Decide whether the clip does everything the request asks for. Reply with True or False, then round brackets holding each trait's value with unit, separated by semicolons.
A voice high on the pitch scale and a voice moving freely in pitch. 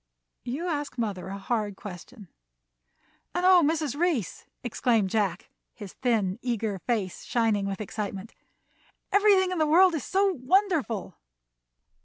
True (240 Hz; 8.2 semitones)